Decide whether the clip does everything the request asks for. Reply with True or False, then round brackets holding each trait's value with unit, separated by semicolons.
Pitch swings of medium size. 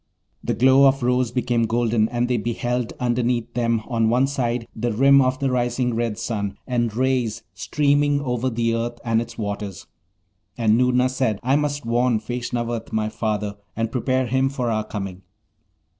False (2.1 semitones)